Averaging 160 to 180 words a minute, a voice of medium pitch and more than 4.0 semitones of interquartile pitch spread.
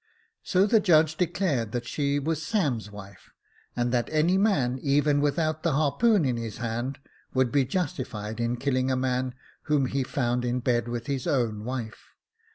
No: average, 170 wpm; low, 130 Hz; average, 4.4 semitones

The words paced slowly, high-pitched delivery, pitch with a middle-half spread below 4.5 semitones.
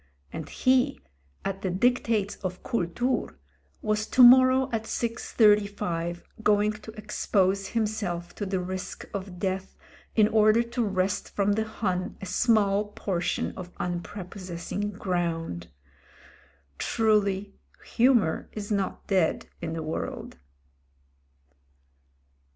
Yes: slow, 120 wpm; high, 200 Hz; average, 3.2 semitones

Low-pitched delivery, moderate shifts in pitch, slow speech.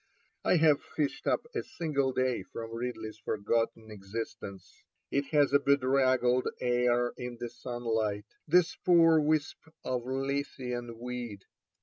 Yes: low, 125 Hz; average, 3.4 semitones; slow, 125 wpm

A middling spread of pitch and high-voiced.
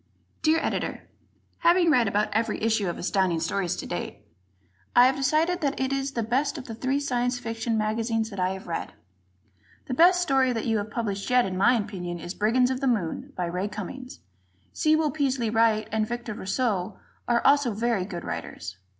Yes: average, 4.4 semitones; high, 230 Hz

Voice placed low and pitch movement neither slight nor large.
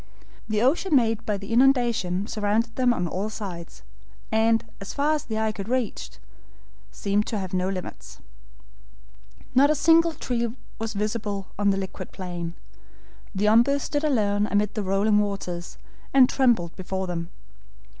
No: high, 210 Hz; average, 3.8 semitones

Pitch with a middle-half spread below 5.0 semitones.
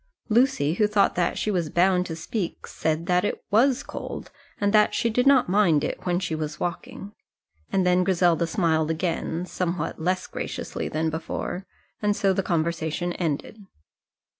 Yes: average, 3.8 semitones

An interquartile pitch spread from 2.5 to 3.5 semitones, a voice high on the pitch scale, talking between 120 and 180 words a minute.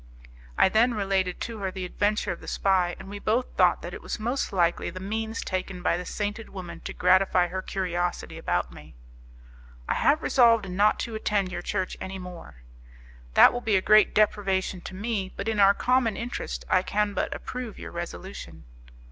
No: average, 2.9 semitones; high, 195 Hz; average, 190 wpm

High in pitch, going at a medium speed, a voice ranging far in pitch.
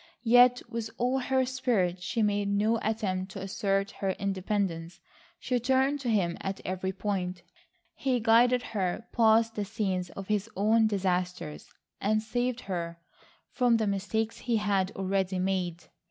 No: high, 205 Hz; average, 150 wpm; average, 3.4 semitones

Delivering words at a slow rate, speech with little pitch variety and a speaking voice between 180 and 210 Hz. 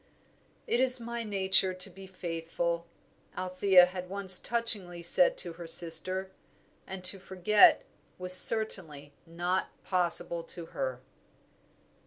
Yes: slow, 120 wpm; narrow, 2.3 semitones; medium, 185 Hz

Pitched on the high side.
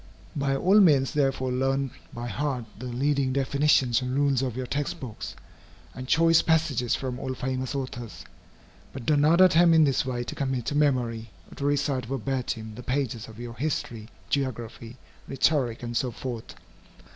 No: low, 130 Hz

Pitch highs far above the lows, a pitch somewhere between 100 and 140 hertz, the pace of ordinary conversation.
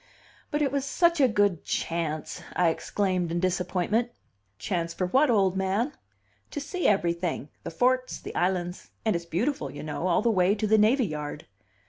No: wide, 5.7 semitones; high, 190 Hz; average, 175 wpm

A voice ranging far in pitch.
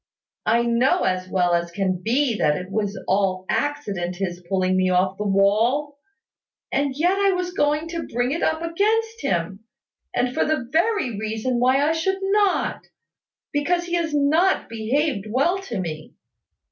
Yes: wide, 8.9 semitones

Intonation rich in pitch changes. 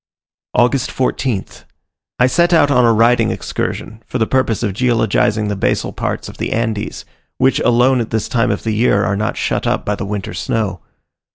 No: average, 3.2 semitones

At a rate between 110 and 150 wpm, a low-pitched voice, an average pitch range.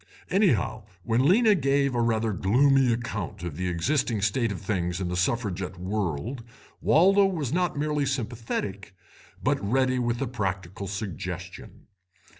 No: average, 140 wpm; low, 115 Hz; wide, 6.0 semitones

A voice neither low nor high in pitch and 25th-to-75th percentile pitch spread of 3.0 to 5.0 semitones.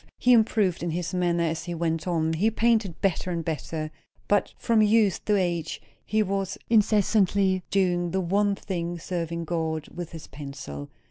Yes: medium, 175 Hz; average, 3.5 semitones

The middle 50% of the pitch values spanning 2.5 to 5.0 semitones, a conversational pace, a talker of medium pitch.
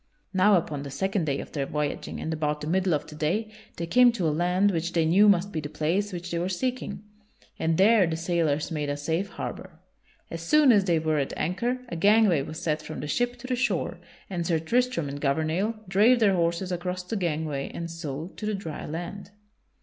No: average, 4.2 semitones; fast, 220 wpm; medium, 170 Hz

